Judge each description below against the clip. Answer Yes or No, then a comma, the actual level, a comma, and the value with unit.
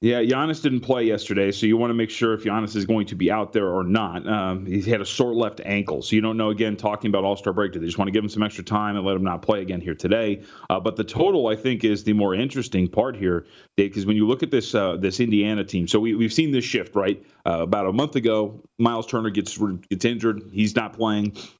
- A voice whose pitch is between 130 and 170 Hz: No, low, 105 Hz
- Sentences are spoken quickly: Yes, fast, 270 wpm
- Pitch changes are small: Yes, narrow, 2.2 semitones